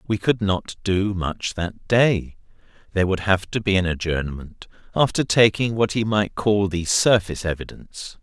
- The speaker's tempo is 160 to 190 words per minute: Yes, average, 170 wpm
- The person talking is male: Yes, male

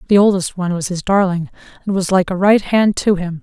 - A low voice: No, high, 190 Hz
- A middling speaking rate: No, fast, 245 wpm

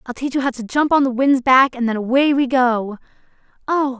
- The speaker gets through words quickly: Yes, fast, 225 wpm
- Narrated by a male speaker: No, female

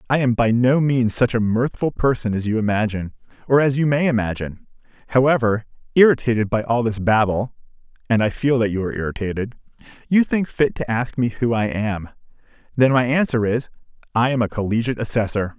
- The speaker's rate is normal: Yes, average, 180 wpm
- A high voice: No, low, 120 Hz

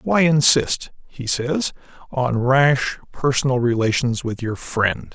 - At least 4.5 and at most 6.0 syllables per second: No, 3.6 syllables/s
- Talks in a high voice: No, low, 125 Hz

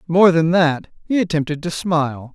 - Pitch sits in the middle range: Yes, medium, 165 Hz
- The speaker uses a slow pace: No, average, 180 wpm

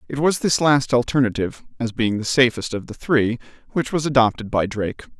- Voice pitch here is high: No, low, 125 Hz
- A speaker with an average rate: Yes, average, 195 wpm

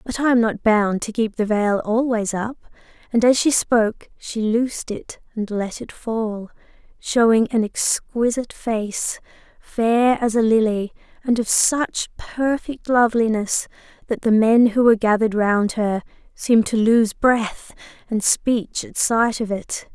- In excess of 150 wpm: Yes, average, 160 wpm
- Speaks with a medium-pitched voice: No, high, 225 Hz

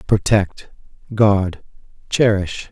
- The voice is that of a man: Yes, male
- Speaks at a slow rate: Yes, slow, 65 wpm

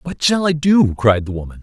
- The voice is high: No, low, 135 Hz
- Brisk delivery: Yes, fast, 260 wpm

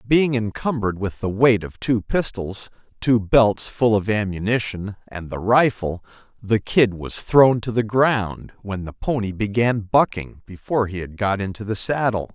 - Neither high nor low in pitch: No, low, 110 Hz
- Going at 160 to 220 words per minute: Yes, average, 170 wpm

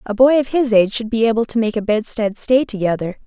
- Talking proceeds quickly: Yes, fast, 255 wpm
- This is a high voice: Yes, high, 225 Hz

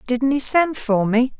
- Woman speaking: Yes, female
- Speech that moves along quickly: Yes, fast, 215 wpm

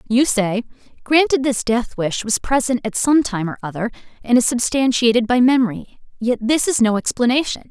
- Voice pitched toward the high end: Yes, high, 240 Hz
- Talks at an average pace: Yes, average, 180 wpm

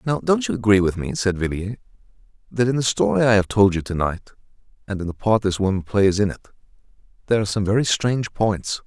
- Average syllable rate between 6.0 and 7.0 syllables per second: Yes, 6.4 syllables/s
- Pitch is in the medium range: No, low, 105 Hz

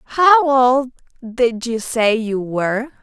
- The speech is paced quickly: No, average, 140 wpm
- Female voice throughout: Yes, female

